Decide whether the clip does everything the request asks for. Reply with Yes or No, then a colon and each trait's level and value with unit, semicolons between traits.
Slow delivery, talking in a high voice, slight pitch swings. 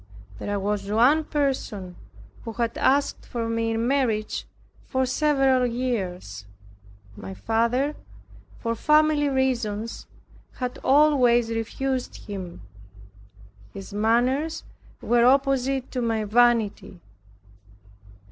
No: slow, 100 wpm; high, 240 Hz; average, 3.7 semitones